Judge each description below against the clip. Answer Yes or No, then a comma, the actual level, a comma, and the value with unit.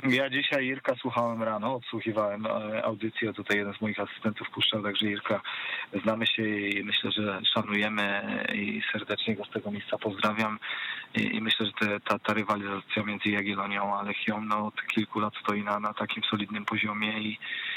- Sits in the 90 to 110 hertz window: Yes, low, 105 Hz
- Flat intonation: Yes, narrow, 1.1 semitones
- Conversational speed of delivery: No, fast, 170 wpm